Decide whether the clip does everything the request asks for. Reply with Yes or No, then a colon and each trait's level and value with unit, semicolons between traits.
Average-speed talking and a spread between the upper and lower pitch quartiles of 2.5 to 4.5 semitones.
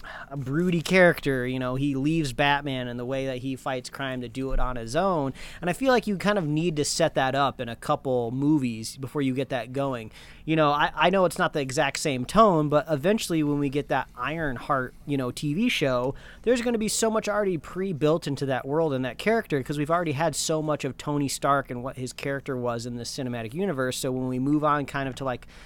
No: fast, 250 wpm; average, 3.6 semitones